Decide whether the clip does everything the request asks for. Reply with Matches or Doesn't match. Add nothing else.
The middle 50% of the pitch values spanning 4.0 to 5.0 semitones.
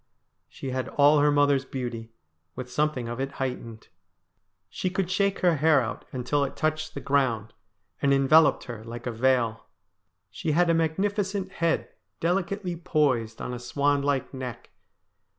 Matches